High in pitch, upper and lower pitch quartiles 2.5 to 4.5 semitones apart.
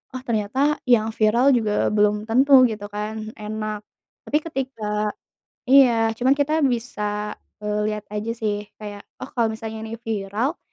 Yes: high, 220 Hz; average, 2.8 semitones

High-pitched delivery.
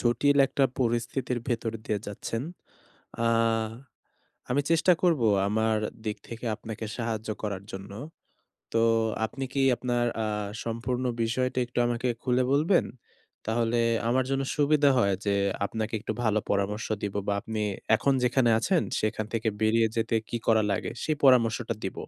No: low, 115 Hz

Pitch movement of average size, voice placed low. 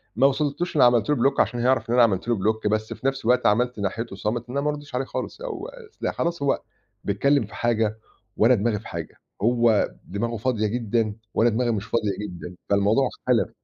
Yes: average, 3.7 semitones; low, 120 Hz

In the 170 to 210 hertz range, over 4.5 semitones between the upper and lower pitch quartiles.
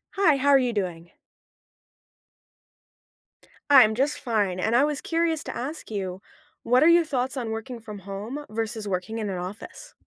No: high, 230 Hz; wide, 5.6 semitones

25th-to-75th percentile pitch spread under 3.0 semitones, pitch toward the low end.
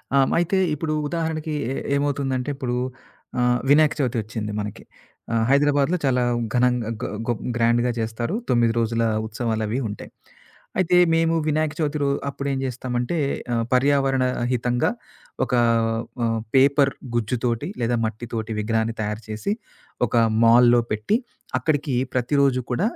No: average, 3.7 semitones; low, 125 Hz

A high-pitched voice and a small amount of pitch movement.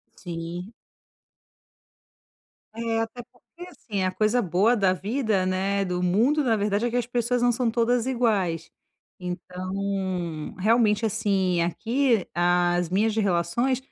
No: high, 205 Hz; average, 4.5 semitones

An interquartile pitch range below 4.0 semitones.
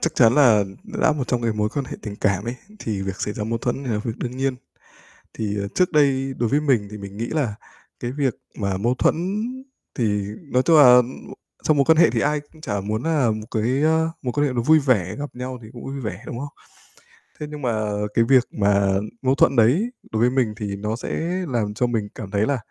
No: average, 4.5 semitones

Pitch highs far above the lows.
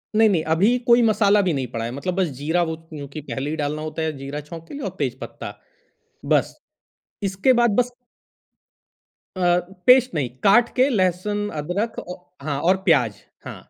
Yes: wide, 6.1 semitones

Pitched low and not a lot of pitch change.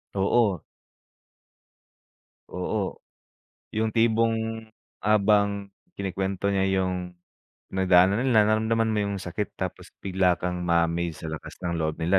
No: very low, 95 Hz; average, 3.3 semitones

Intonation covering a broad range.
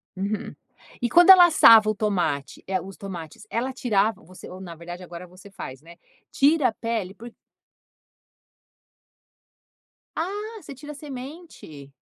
Yes: wide, 7.3 semitones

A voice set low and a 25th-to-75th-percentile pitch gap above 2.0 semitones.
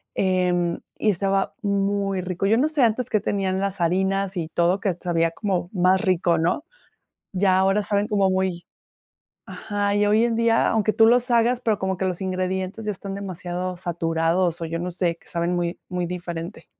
No: high, 190 Hz; narrow, 2.5 semitones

